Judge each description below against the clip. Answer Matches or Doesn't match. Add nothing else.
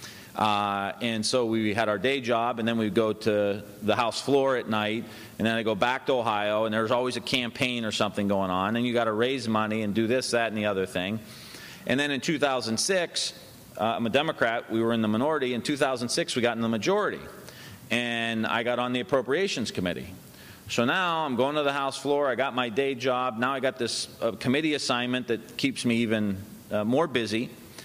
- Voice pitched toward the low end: Matches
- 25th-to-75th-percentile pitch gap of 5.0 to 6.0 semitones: Doesn't match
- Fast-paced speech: Matches